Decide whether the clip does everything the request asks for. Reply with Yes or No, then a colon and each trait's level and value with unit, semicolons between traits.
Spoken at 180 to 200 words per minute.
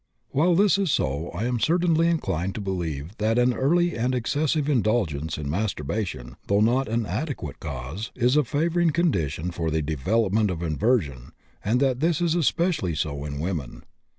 No: average, 170 wpm